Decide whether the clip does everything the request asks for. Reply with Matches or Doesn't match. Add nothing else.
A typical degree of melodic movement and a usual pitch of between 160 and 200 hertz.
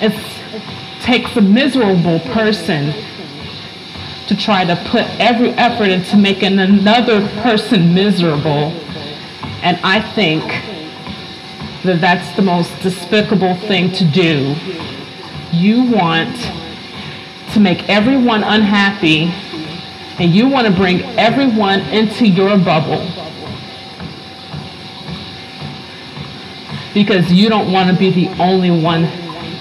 Matches